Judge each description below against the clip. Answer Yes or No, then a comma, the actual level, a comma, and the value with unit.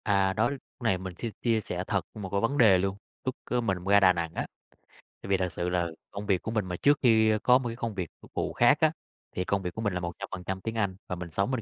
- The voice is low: Yes, low, 100 Hz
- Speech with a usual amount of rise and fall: Yes, average, 3.9 semitones